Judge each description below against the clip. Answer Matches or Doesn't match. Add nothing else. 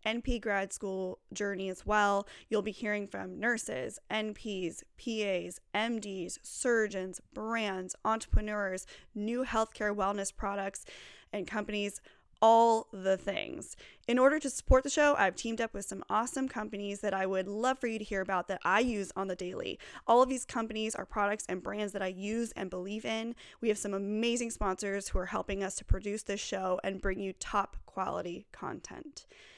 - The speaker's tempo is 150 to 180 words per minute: Matches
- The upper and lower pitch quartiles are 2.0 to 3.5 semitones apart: Matches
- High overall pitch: Matches